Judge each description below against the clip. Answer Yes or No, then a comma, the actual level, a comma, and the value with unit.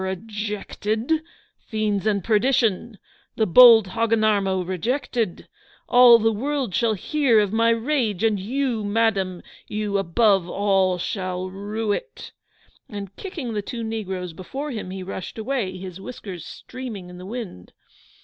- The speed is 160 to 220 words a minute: No, average, 150 wpm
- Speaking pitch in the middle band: No, high, 215 Hz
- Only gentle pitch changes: No, average, 3.4 semitones